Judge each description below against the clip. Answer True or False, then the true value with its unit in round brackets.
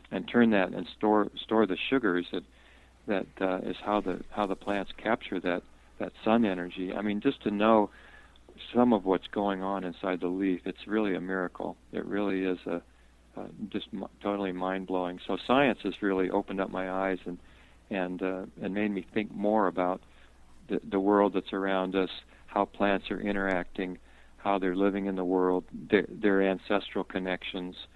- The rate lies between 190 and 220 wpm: False (180 wpm)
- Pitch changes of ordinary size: False (1.9 semitones)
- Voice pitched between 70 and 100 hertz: True (95 Hz)